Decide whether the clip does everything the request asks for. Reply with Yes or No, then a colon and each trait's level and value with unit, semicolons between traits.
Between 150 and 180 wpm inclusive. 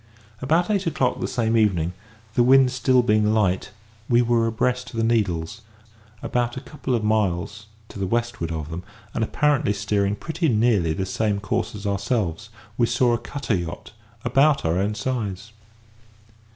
Yes: average, 165 wpm